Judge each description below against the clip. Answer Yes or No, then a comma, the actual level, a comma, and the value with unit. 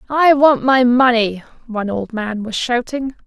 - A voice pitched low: No, high, 240 Hz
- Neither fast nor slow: Yes, average, 165 wpm